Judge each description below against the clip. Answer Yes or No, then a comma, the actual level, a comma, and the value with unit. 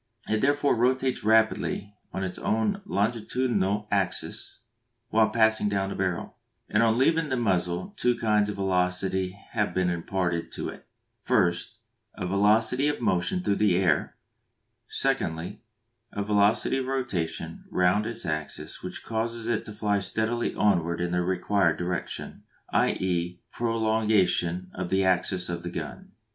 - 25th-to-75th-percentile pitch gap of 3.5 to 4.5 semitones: Yes, average, 3.9 semitones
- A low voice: Yes, low, 100 Hz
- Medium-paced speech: Yes, average, 145 wpm